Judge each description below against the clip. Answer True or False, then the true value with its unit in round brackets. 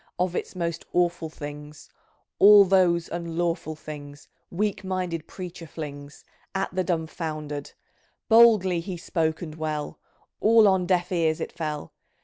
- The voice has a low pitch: False (170 Hz)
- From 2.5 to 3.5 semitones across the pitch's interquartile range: True (3.0 semitones)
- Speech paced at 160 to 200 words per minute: False (135 wpm)